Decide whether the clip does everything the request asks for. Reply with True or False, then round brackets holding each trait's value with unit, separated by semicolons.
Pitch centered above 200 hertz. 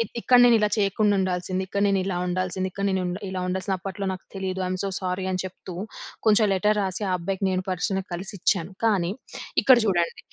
False (190 Hz)